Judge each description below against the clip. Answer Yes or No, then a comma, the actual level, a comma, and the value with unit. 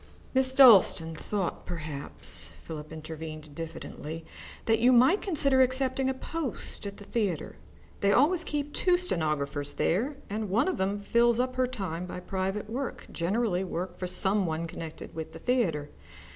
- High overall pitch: Yes, high, 200 Hz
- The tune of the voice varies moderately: No, wide, 7.7 semitones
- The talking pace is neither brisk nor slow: Yes, average, 160 wpm